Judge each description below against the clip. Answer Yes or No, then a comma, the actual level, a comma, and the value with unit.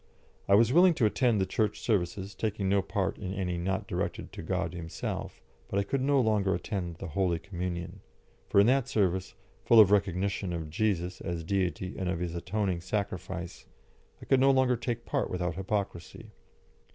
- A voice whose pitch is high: No, very low, 95 Hz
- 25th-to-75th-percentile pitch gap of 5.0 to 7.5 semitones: No, average, 3.4 semitones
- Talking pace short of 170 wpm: No, average, 180 wpm